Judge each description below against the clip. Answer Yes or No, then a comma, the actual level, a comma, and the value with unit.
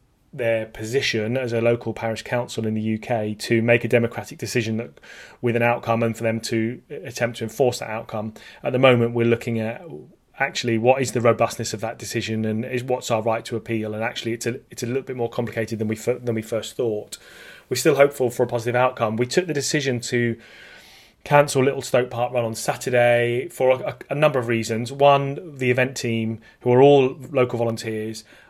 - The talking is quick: Yes, fast, 210 wpm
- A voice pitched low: Yes, low, 120 Hz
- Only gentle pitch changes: Yes, narrow, 2.0 semitones